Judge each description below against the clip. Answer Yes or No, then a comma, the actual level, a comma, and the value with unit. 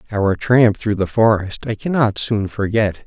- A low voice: Yes, low, 110 Hz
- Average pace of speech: Yes, average, 175 wpm